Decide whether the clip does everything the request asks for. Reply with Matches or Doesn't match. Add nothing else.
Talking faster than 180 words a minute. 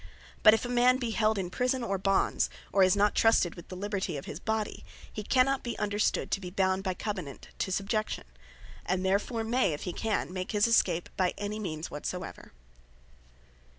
Matches